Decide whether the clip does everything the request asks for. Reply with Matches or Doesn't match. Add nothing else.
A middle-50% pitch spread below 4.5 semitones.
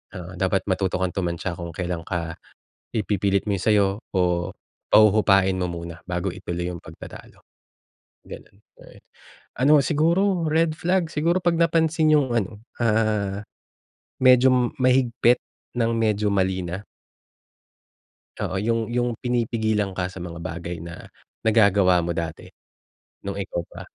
Doesn't match